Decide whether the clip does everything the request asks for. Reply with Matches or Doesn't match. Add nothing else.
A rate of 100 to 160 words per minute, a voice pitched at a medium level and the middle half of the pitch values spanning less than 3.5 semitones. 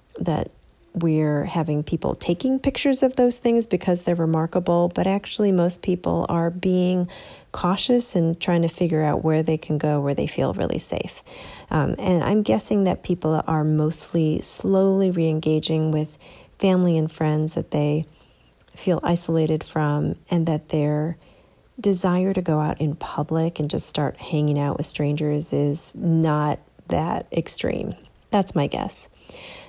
Matches